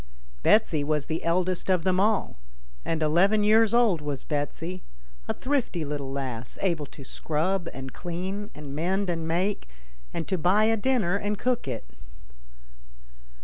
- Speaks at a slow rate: No, average, 150 wpm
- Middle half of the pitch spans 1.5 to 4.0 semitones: No, average, 5.2 semitones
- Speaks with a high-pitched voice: No, medium, 175 Hz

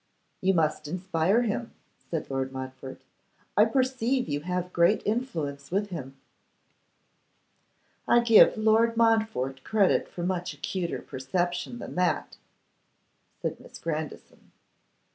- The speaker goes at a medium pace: No, slow, 115 wpm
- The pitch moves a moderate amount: No, wide, 6.5 semitones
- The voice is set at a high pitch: No, medium, 180 Hz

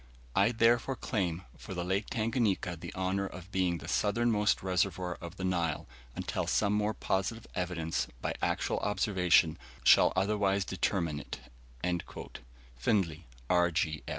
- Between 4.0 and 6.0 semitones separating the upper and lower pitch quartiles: No, average, 3.0 semitones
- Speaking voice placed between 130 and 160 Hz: No, very low, 95 Hz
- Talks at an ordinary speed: No, slow, 125 wpm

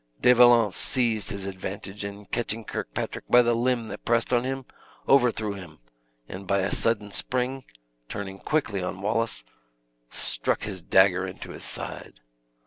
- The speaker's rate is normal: Yes, average, 150 wpm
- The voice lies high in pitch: No, low, 105 Hz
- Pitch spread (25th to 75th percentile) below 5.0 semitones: Yes, average, 3.8 semitones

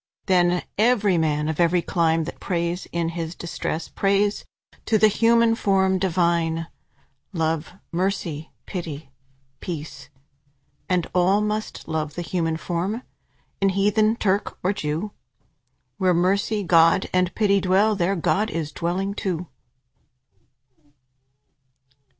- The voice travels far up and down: No, average, 3.2 semitones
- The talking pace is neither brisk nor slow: No, slow, 120 wpm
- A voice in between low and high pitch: Yes, medium, 180 Hz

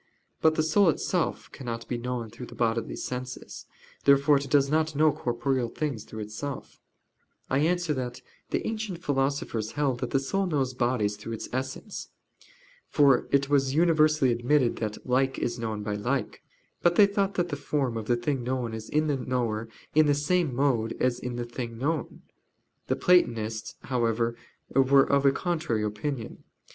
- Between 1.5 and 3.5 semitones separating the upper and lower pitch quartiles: No, average, 4.0 semitones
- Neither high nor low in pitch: No, low, 130 Hz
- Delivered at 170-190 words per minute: Yes, average, 175 wpm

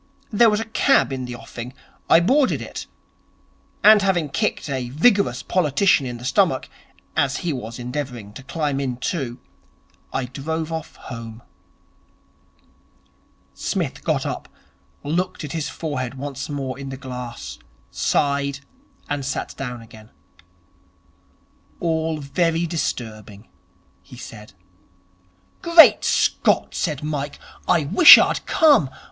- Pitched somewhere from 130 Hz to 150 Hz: Yes, medium, 140 Hz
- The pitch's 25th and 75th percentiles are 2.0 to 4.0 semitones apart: No, average, 4.8 semitones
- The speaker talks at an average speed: No, slow, 125 wpm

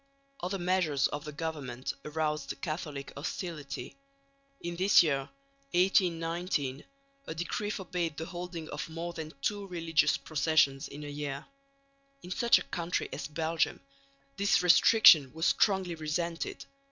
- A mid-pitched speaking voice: Yes, medium, 165 Hz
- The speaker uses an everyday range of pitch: Yes, average, 3.1 semitones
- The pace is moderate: No, slow, 130 wpm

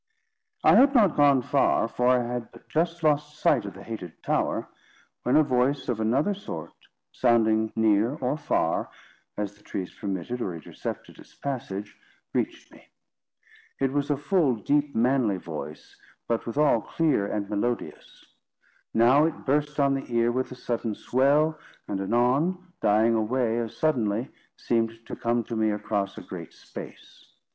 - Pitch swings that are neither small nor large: Yes, average, 4.7 semitones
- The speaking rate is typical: Yes, average, 160 wpm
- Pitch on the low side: Yes, low, 125 Hz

